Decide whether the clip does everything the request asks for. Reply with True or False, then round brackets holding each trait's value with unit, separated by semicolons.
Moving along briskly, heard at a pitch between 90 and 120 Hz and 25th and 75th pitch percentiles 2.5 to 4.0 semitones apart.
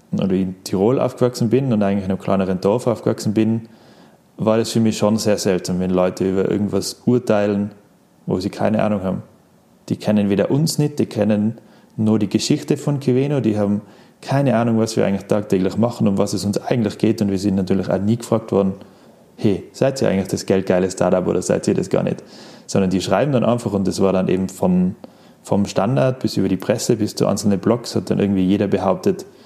True (215 wpm; 105 Hz; 2.8 semitones)